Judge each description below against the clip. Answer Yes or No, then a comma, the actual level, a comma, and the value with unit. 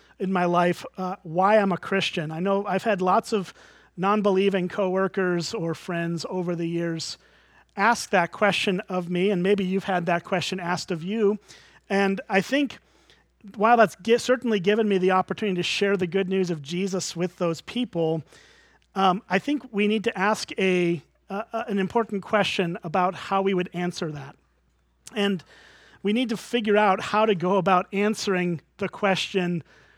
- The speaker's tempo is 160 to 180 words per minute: Yes, average, 175 wpm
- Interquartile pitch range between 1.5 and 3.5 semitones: Yes, narrow, 2.5 semitones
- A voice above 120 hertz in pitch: Yes, high, 190 Hz